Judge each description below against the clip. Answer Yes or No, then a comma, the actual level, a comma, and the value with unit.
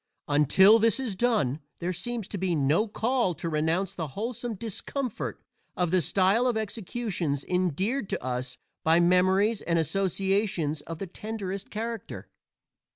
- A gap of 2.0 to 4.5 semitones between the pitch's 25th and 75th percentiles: No, average, 4.9 semitones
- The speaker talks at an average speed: Yes, average, 145 wpm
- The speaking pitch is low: No, high, 190 Hz